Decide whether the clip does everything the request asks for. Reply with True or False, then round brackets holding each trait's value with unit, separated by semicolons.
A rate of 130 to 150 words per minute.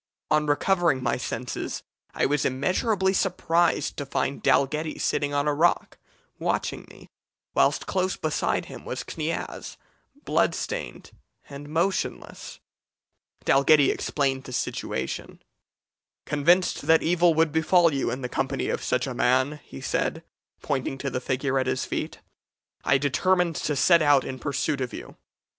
True (145 wpm)